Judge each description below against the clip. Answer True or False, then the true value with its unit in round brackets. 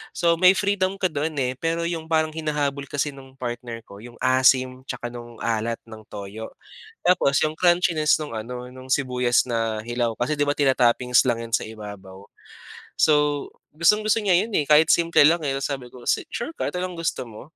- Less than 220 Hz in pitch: True (135 Hz)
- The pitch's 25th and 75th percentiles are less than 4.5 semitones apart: False (5.2 semitones)